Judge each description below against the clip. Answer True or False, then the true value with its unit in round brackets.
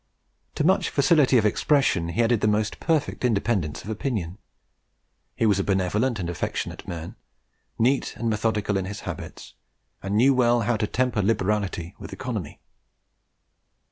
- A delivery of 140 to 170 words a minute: True (150 wpm)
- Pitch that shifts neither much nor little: True (4.1 semitones)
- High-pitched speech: False (110 Hz)